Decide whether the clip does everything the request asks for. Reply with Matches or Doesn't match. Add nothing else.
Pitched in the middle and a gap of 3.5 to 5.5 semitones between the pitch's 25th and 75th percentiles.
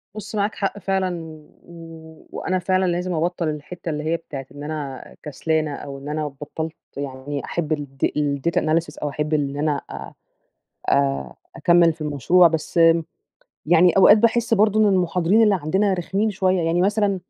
Matches